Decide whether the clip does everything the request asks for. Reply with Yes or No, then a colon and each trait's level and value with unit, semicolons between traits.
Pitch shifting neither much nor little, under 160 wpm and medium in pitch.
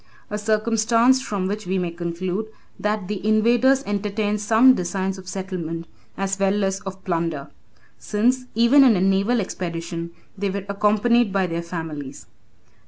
No: average, 3.2 semitones; average, 150 wpm; high, 195 Hz